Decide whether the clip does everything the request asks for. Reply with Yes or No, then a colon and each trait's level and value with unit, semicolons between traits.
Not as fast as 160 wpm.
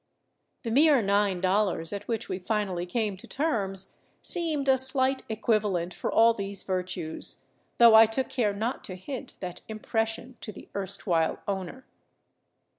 Yes: average, 150 wpm